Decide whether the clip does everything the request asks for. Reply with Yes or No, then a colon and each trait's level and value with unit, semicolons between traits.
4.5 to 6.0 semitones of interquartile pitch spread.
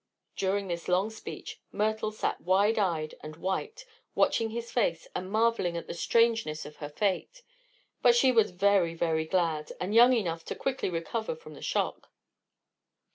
Yes: average, 5.2 semitones